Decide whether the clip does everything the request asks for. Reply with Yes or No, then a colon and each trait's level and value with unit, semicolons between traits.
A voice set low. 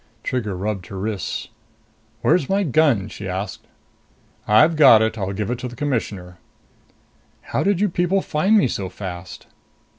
Yes: low, 110 Hz